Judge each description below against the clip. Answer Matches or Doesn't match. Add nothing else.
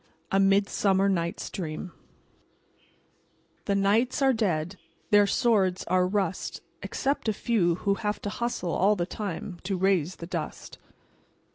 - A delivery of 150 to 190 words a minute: Doesn't match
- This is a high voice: Matches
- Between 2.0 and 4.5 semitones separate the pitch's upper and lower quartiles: Matches